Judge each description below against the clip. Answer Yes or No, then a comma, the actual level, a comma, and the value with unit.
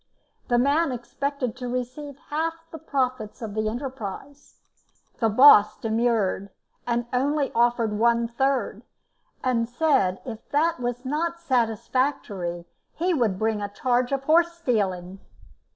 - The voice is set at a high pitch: Yes, high, 245 Hz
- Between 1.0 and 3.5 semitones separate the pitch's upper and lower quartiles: No, average, 4.2 semitones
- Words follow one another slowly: Yes, slow, 130 wpm